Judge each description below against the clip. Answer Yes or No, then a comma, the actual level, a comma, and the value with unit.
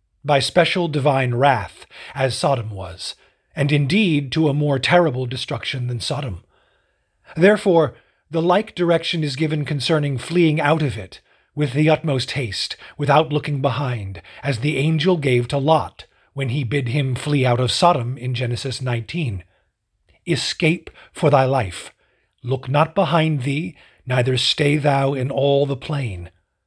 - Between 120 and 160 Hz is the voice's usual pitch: Yes, medium, 140 Hz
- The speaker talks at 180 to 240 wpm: No, average, 150 wpm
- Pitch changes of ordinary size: Yes, average, 3.4 semitones